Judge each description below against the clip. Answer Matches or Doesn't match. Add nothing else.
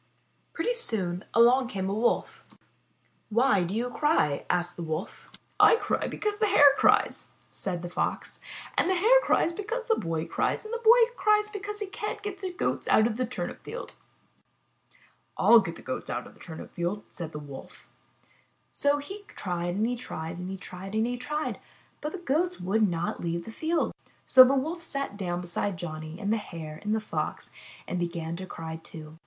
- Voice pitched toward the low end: Doesn't match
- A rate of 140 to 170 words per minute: Doesn't match